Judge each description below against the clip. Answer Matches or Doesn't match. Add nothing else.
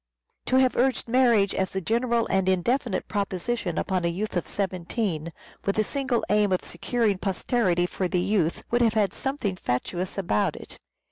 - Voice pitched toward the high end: Matches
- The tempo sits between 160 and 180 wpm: Matches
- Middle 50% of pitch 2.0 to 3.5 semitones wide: Doesn't match